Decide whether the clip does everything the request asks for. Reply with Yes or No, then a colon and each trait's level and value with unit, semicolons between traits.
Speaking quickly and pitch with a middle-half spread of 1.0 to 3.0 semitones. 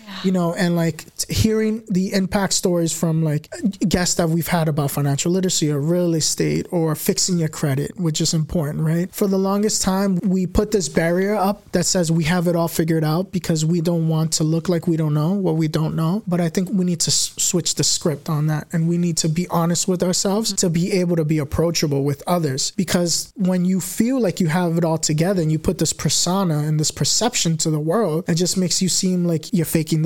Yes: fast, 230 wpm; average, 2.7 semitones